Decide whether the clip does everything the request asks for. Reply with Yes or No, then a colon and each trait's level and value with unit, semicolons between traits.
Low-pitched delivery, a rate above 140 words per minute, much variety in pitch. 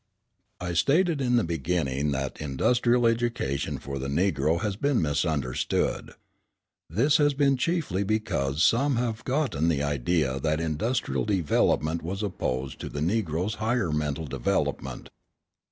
No: very low, 85 Hz; slow, 135 wpm; wide, 8.4 semitones